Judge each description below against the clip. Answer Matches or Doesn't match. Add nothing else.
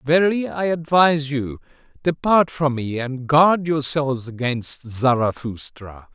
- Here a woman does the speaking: Doesn't match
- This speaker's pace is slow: Matches